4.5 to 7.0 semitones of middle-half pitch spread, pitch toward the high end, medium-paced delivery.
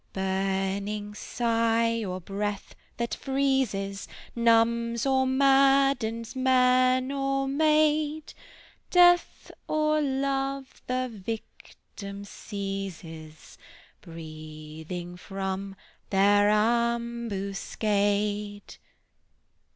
No: average, 5.2 semitones; high, 225 Hz; slow, 65 wpm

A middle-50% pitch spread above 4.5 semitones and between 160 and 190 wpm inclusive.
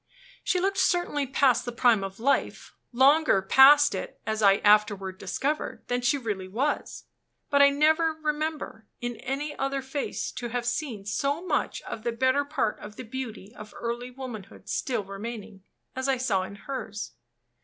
Yes: average, 4.9 semitones; average, 165 wpm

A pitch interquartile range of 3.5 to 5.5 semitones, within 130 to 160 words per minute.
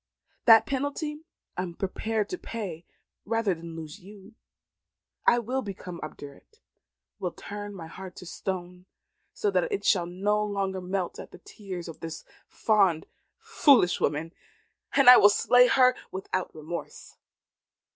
Yes: average, 4.7 semitones; average, 145 wpm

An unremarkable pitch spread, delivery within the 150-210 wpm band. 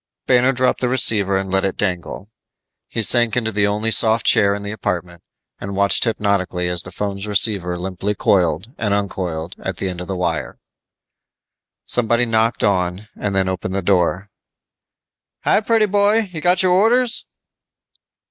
Yes: average, 4.1 semitones; average, 160 wpm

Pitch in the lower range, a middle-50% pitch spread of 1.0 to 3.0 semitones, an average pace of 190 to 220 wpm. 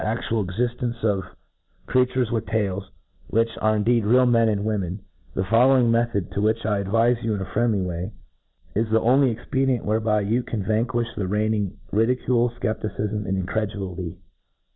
No: low, 110 Hz; average, 2.7 semitones; average, 165 wpm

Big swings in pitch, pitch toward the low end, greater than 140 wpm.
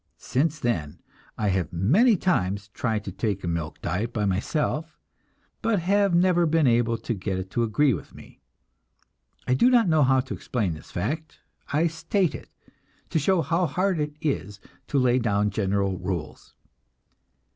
Yes: wide, 8.7 semitones; low, 125 Hz; average, 165 wpm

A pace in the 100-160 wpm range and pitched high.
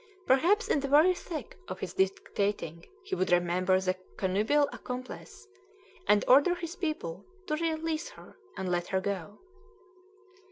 Yes: average, 145 wpm; high, 210 Hz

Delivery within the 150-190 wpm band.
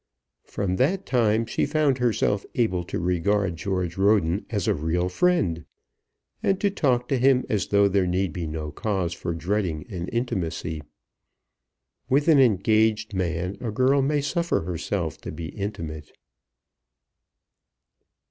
No: average, 140 wpm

